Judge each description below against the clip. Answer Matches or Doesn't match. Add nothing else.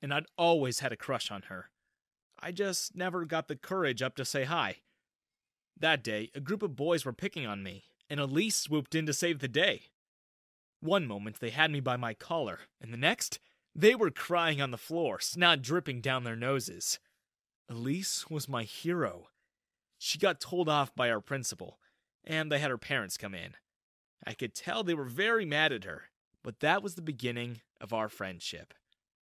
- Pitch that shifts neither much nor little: Doesn't match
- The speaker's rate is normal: Matches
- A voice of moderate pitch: Matches